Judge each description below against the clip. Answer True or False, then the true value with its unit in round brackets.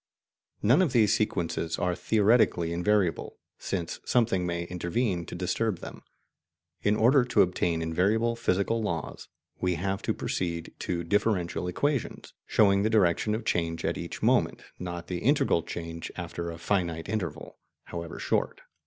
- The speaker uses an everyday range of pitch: True (4.2 semitones)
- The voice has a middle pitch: False (90 Hz)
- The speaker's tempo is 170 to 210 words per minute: False (145 wpm)